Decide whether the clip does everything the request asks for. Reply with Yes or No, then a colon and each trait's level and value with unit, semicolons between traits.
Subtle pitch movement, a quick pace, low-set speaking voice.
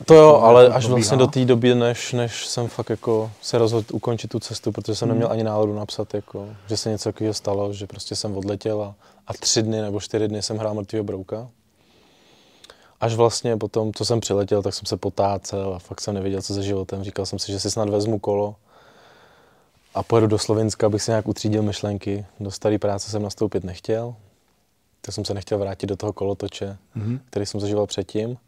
Yes: narrow, 2.0 semitones; fast, 205 wpm; low, 105 Hz